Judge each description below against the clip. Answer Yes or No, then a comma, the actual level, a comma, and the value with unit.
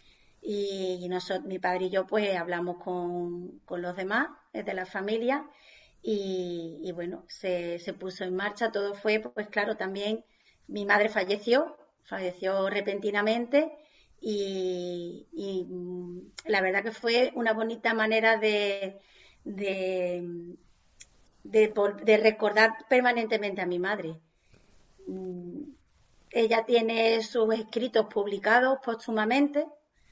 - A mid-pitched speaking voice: No, high, 205 Hz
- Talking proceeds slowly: Yes, slow, 115 wpm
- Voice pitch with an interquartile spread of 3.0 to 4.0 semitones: Yes, average, 3.5 semitones